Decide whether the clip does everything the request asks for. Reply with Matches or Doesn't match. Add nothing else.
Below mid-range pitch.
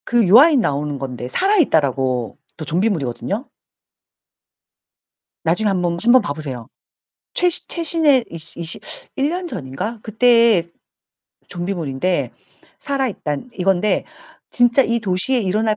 Doesn't match